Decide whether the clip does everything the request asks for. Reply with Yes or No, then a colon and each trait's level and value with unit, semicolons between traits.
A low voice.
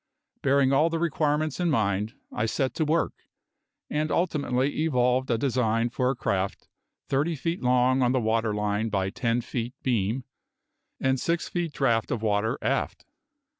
Yes: low, 125 Hz